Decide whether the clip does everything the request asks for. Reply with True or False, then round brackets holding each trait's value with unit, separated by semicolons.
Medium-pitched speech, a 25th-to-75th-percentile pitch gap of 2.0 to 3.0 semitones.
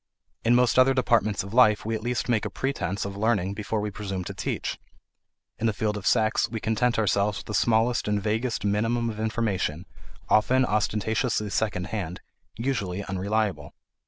False (110 Hz; 2.4 semitones)